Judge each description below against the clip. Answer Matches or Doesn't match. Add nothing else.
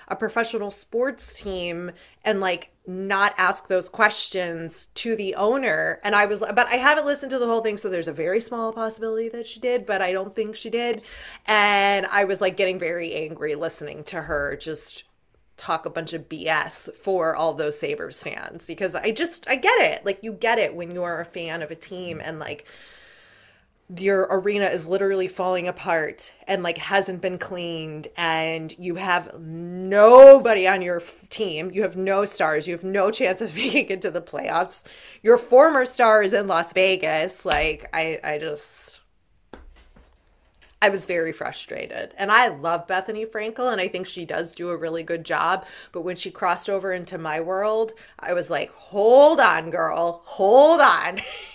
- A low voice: Doesn't match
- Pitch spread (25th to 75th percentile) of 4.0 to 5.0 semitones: Matches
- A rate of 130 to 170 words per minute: Doesn't match